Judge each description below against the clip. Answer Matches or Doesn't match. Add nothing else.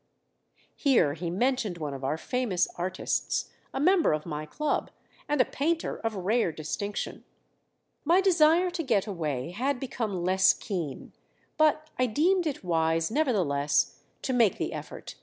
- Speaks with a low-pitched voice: Doesn't match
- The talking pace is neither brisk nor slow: Matches